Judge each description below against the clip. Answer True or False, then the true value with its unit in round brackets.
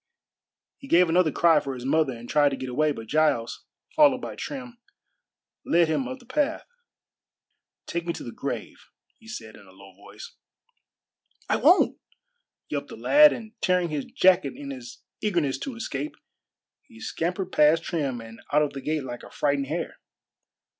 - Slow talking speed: False (175 wpm)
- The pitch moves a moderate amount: False (8.7 semitones)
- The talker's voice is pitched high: False (160 Hz)